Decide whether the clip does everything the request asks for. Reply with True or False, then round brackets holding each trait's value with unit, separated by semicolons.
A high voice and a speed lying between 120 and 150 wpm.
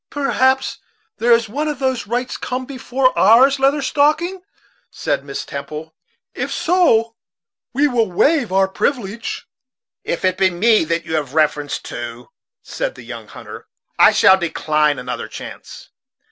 True (225 Hz; 145 wpm)